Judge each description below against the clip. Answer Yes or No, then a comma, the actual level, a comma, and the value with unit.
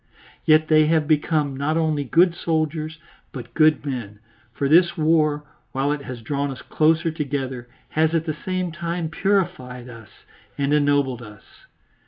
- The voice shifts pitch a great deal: No, average, 2.8 semitones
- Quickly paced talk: No, average, 155 wpm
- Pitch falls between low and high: Yes, medium, 155 Hz